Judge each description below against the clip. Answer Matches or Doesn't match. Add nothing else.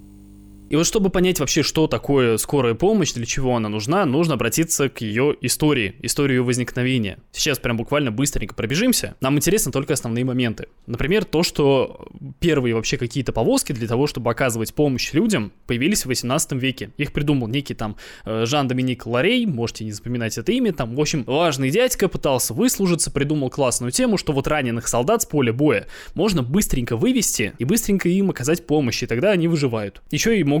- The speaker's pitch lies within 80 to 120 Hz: Doesn't match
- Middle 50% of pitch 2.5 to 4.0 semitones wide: Doesn't match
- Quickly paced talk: Matches